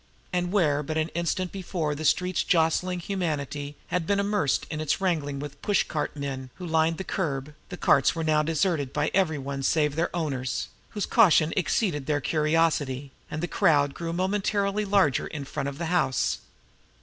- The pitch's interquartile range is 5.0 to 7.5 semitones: No, average, 3.9 semitones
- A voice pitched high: No, medium, 160 Hz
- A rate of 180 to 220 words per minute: Yes, average, 185 wpm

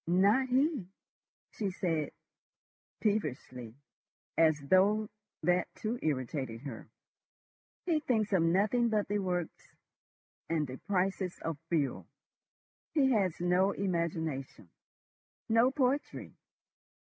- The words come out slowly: Yes, slow, 100 wpm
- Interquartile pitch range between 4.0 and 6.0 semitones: Yes, wide, 5.5 semitones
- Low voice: No, medium, 185 Hz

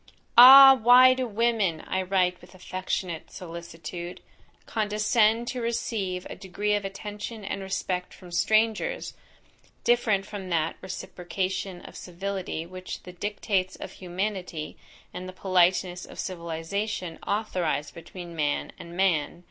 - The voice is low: No, high, 190 Hz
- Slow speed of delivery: Yes, slow, 125 wpm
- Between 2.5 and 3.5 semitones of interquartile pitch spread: Yes, average, 3.1 semitones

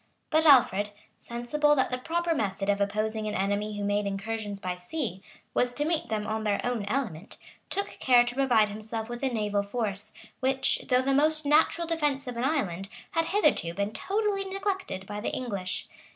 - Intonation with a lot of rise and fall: Yes, wide, 6.3 semitones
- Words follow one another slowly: No, average, 190 wpm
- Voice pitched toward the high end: Yes, high, 235 Hz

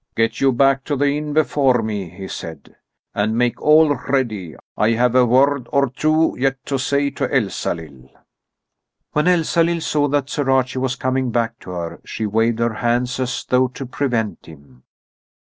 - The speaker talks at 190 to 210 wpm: No, average, 175 wpm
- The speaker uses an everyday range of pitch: Yes, average, 3.9 semitones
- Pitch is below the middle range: Yes, low, 130 Hz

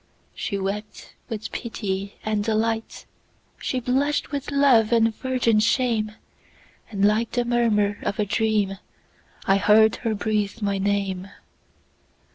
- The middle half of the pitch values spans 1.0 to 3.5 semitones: Yes, narrow, 2.4 semitones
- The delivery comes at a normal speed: No, slow, 110 wpm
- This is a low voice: No, high, 215 Hz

